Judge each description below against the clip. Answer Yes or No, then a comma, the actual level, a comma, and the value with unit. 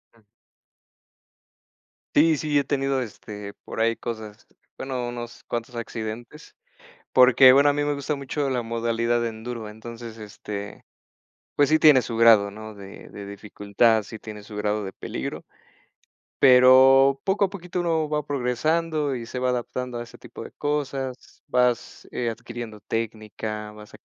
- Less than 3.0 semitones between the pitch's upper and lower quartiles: No, average, 3.8 semitones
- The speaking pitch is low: Yes, low, 120 Hz